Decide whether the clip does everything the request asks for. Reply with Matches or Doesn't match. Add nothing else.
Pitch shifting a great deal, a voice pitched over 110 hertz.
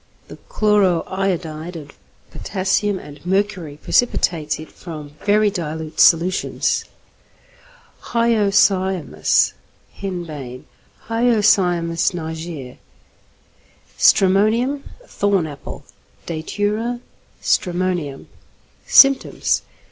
Doesn't match